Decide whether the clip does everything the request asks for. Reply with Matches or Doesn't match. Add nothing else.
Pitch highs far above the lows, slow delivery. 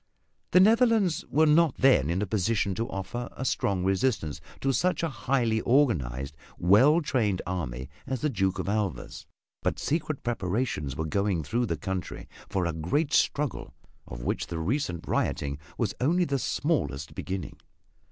Doesn't match